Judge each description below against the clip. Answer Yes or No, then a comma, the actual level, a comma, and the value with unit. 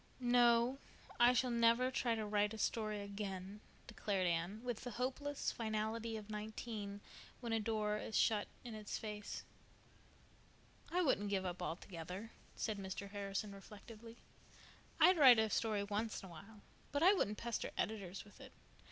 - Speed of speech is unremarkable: Yes, average, 160 wpm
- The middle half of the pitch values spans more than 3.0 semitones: No, narrow, 2.6 semitones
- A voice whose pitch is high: Yes, high, 215 Hz